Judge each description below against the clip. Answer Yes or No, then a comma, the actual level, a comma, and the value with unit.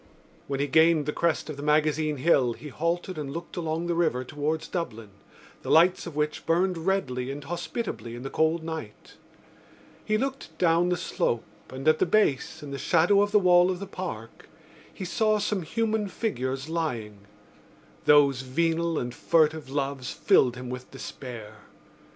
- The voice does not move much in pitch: No, average, 4.5 semitones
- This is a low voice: No, medium, 155 Hz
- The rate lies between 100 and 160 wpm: No, average, 170 wpm